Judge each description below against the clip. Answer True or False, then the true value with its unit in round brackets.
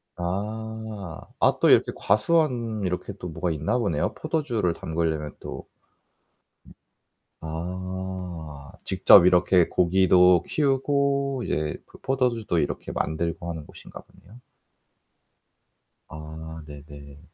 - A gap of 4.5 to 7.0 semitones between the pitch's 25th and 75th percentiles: True (5.6 semitones)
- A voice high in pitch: False (90 Hz)